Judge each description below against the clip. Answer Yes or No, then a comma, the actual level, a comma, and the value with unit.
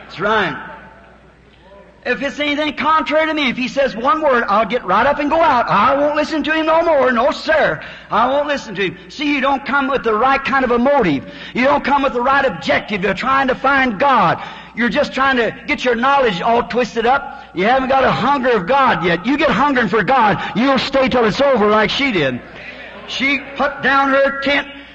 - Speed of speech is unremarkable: No, fast, 225 wpm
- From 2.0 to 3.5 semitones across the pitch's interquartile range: Yes, average, 2.9 semitones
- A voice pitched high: Yes, very high, 270 Hz